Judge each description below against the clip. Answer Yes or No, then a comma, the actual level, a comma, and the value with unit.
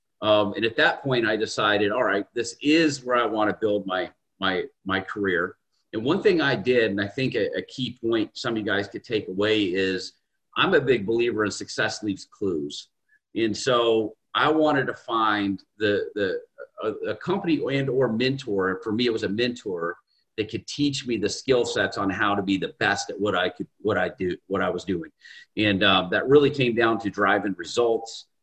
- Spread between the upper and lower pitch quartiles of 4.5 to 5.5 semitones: Yes, average, 5.1 semitones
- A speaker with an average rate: No, fast, 215 wpm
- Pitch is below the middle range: Yes, low, 115 Hz